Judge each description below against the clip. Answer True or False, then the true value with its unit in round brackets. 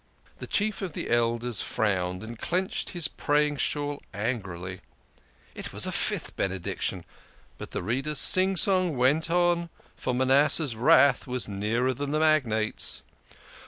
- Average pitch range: False (6.1 semitones)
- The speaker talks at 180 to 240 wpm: False (145 wpm)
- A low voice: True (130 Hz)